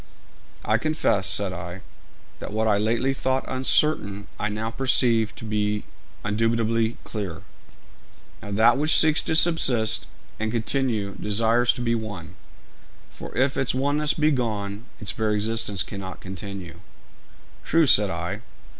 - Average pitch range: Yes, average, 4.0 semitones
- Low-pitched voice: Yes, low, 110 Hz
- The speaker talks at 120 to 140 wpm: Yes, slow, 135 wpm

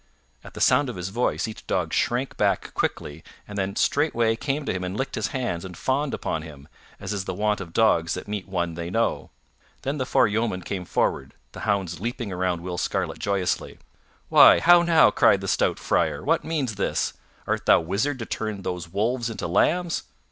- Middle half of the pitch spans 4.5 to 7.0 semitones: Yes, wide, 5.4 semitones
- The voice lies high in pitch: No, low, 105 Hz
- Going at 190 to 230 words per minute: Yes, average, 200 wpm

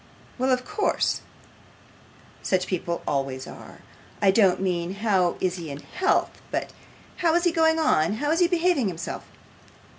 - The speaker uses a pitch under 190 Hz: No, high, 200 Hz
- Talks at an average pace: Yes, average, 155 wpm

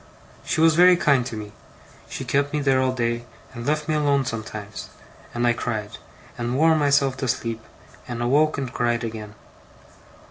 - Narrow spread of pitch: No, average, 3.7 semitones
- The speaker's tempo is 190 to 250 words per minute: No, average, 175 wpm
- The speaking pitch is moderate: No, low, 130 Hz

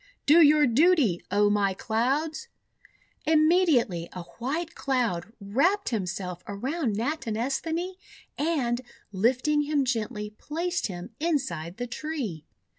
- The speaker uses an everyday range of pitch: No, wide, 7.0 semitones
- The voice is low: No, very high, 255 Hz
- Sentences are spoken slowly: Yes, slow, 115 wpm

